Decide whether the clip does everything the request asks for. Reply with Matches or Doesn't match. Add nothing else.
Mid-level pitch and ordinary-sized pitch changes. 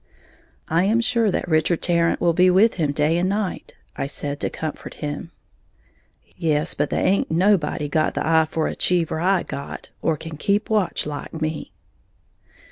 Matches